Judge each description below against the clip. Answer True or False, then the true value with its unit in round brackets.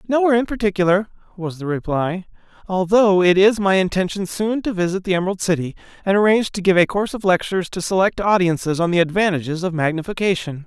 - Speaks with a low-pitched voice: False (190 Hz)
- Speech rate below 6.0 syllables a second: False (6.4 syllables/s)